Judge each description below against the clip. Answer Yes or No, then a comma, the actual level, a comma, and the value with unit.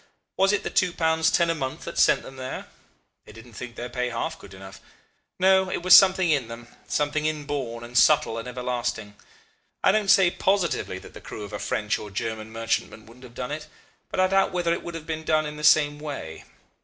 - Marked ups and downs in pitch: Yes, wide, 6.2 semitones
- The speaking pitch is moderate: Yes, medium, 145 Hz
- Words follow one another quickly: Yes, fast, 220 wpm